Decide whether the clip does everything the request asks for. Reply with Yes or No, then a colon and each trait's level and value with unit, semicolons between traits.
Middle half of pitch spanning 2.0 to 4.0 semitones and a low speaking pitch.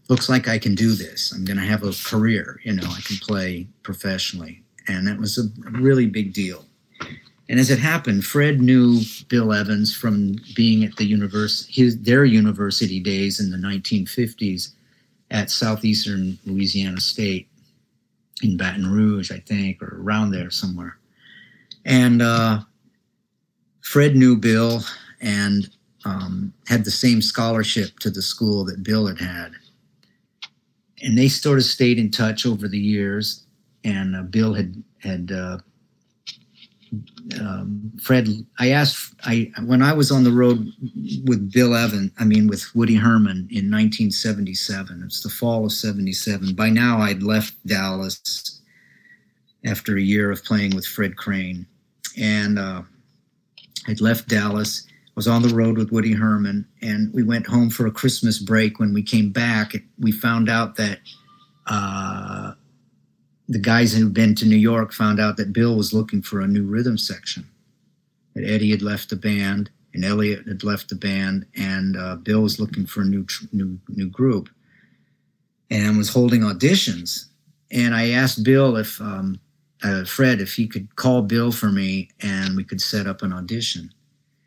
Yes: average, 2.8 semitones; low, 105 Hz